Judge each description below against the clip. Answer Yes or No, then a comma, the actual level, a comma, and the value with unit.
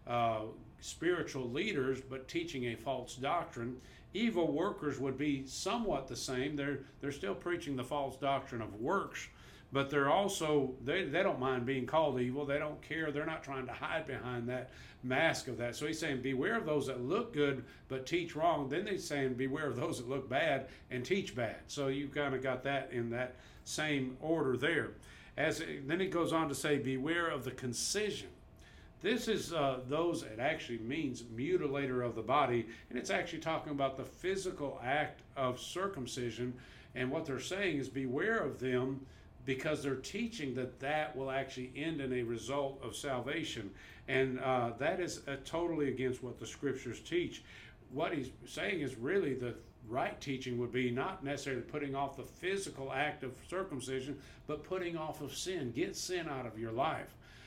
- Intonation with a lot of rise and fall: No, average, 3.3 semitones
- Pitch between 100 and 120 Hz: No, low, 135 Hz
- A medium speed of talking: Yes, average, 185 wpm